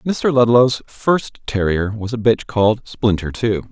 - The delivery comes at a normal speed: Yes, average, 160 wpm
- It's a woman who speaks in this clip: No, male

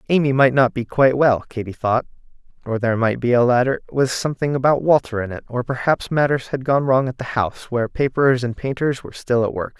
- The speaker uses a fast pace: Yes, fast, 225 wpm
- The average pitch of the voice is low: Yes, low, 125 Hz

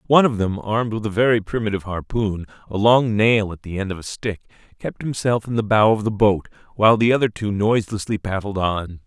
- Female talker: No, male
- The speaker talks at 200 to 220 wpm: Yes, fast, 205 wpm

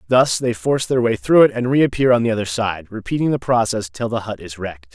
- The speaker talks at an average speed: No, fast, 255 wpm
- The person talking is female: No, male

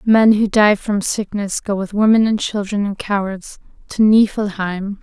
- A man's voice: No, female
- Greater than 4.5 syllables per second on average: No, 4.1 syllables/s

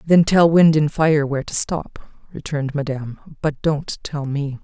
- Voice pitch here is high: No, medium, 150 Hz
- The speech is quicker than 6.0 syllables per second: No, 4.5 syllables/s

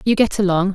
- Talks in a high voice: Yes, high, 195 Hz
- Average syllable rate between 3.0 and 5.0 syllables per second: No, 6.4 syllables/s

